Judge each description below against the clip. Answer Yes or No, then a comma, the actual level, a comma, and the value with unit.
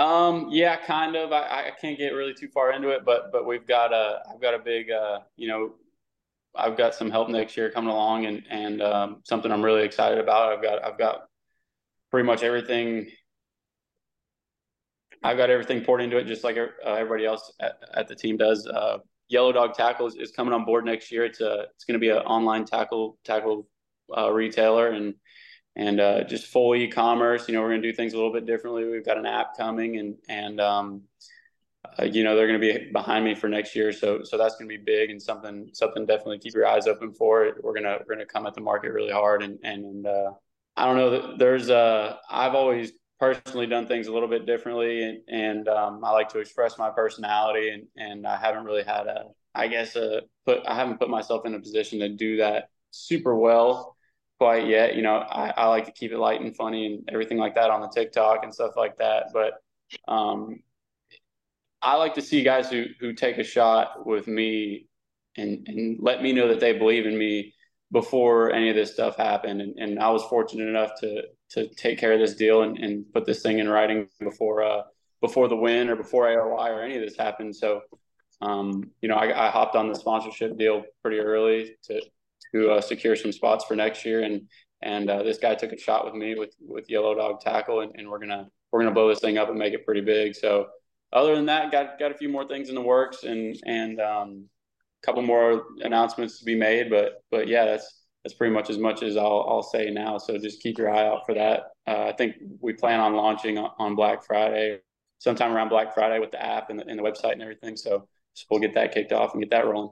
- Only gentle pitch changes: Yes, narrow, 1.8 semitones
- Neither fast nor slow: No, fast, 230 wpm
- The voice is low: Yes, low, 110 Hz